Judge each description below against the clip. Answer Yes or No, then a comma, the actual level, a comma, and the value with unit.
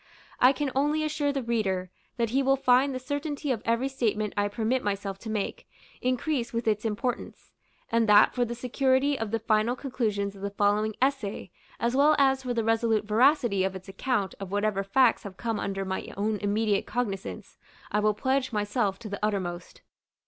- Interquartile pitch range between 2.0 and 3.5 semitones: No, average, 4.2 semitones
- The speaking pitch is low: No, high, 225 Hz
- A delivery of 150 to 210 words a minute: Yes, average, 190 wpm